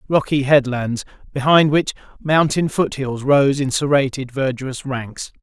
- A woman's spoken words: No, male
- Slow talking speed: Yes, slow, 120 wpm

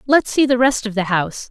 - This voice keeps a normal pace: No, fast, 280 wpm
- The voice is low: No, high, 235 Hz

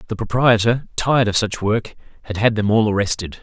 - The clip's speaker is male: Yes, male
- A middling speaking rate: Yes, average, 195 wpm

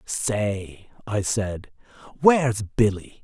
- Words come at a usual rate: No, slow, 95 wpm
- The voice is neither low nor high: No, low, 110 Hz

